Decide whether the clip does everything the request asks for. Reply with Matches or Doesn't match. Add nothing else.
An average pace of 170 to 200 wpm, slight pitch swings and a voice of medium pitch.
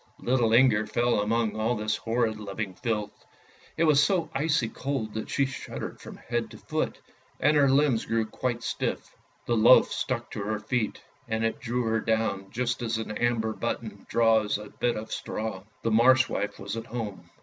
Doesn't match